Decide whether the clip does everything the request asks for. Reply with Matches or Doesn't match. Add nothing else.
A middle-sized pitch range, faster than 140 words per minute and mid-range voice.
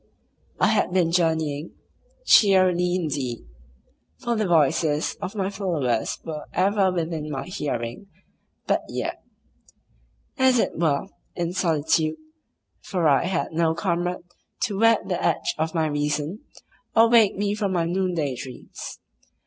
Doesn't match